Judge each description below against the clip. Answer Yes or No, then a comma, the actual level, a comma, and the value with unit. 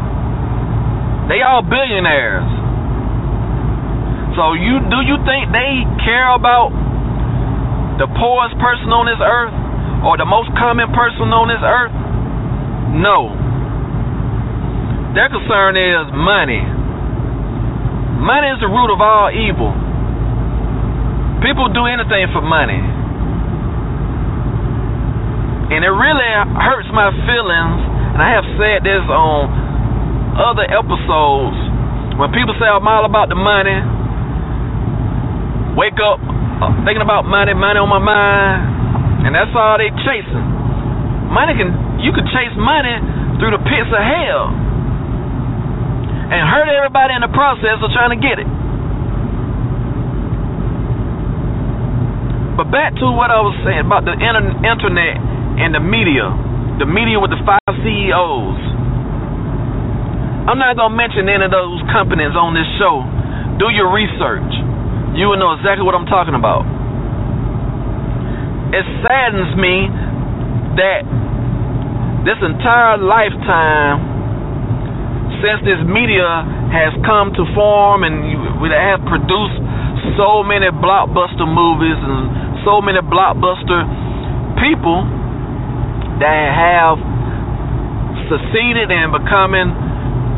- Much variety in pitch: Yes, wide, 7.4 semitones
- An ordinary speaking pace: No, slow, 115 wpm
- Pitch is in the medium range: No, low, 130 Hz